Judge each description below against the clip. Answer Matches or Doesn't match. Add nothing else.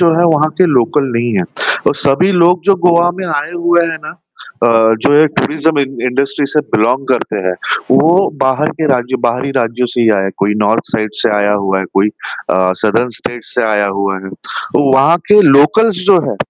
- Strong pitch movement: Matches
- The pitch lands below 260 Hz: Matches